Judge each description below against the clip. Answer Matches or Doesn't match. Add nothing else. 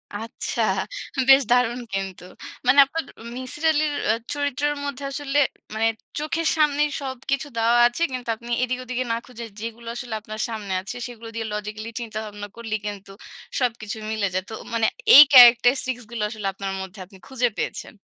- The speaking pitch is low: Doesn't match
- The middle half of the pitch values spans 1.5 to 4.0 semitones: Matches